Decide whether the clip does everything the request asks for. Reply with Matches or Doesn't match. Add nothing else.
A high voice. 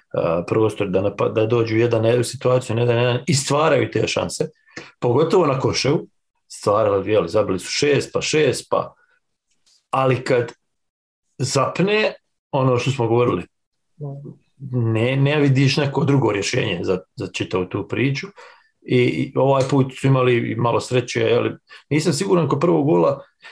Doesn't match